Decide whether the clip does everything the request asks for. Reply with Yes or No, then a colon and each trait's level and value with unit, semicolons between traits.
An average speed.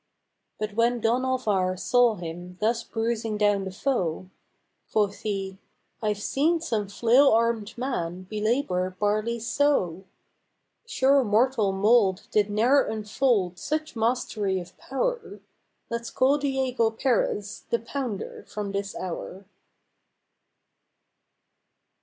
No: slow, 115 wpm